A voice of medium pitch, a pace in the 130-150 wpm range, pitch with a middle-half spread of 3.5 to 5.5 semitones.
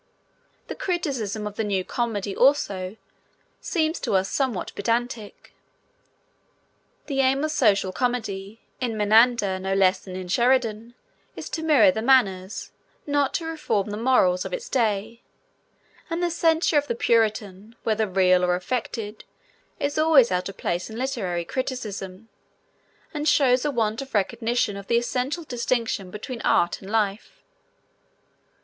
No: high, 225 Hz; average, 145 wpm; average, 5.0 semitones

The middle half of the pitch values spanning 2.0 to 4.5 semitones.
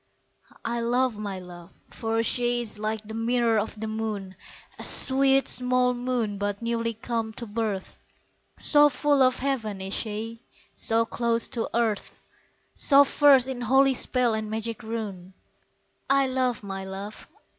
Yes: average, 2.8 semitones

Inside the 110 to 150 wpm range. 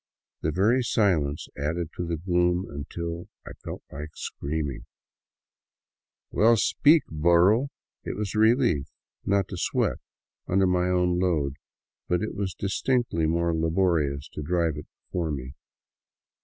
Yes: average, 140 wpm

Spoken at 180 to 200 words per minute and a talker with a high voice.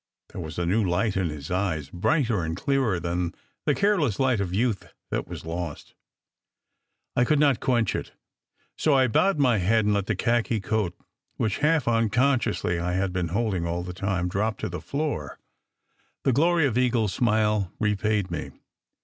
No: average, 185 wpm; low, 105 Hz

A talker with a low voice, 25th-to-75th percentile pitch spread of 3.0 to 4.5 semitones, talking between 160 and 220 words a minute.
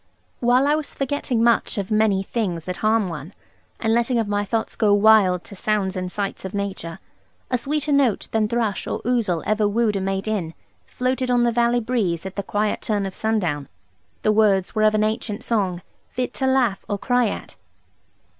No: high, 215 Hz; average, 3.5 semitones; average, 195 wpm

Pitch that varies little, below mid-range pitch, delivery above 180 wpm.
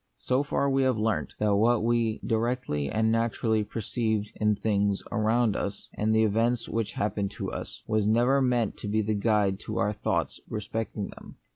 Yes: narrow, 2.1 semitones; low, 110 Hz; average, 190 wpm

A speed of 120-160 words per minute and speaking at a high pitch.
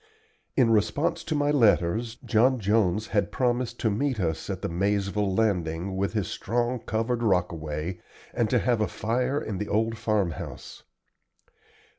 No: average, 150 wpm; low, 110 Hz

